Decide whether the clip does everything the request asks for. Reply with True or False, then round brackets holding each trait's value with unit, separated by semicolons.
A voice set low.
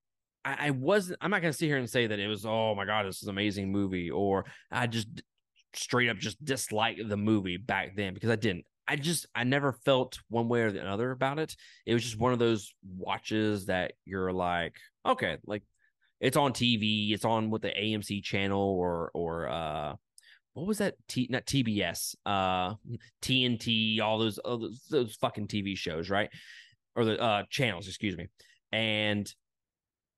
True (110 Hz)